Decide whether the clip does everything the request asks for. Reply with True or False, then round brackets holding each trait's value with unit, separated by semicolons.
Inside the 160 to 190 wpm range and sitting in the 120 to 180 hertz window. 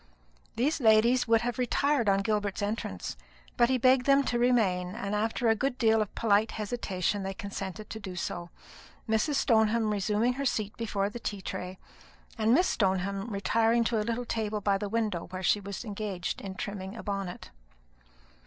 False (180 wpm; 215 Hz)